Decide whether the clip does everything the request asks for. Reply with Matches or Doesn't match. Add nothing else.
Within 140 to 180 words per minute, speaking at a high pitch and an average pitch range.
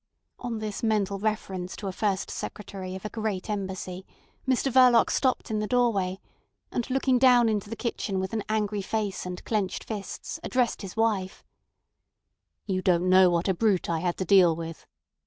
Matches